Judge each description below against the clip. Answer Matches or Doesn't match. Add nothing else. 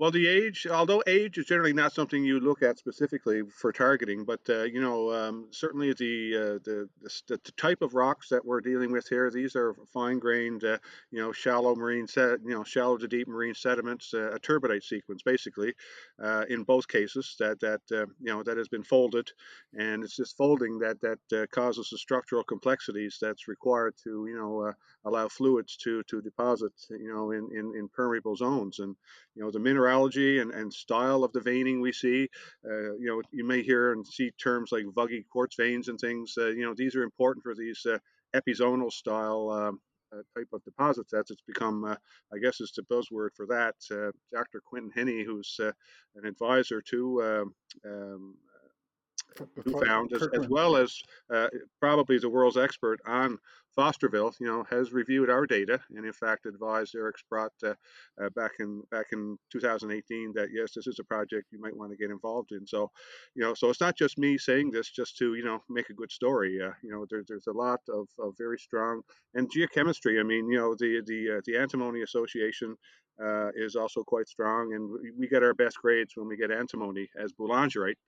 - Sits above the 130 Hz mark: Doesn't match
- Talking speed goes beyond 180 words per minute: Matches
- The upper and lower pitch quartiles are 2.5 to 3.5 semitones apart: Matches